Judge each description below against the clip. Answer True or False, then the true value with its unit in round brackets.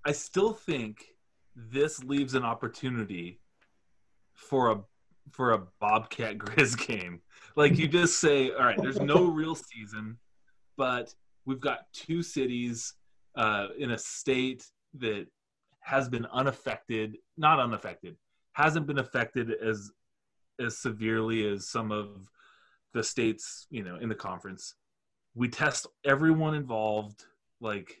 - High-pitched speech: False (125 Hz)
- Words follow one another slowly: True (130 wpm)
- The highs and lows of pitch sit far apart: False (5.0 semitones)